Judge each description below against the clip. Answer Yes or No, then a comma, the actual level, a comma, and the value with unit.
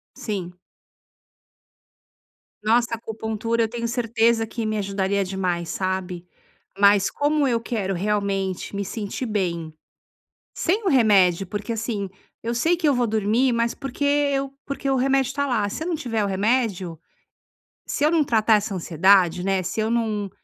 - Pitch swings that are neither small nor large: Yes, average, 3.9 semitones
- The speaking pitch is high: Yes, high, 220 Hz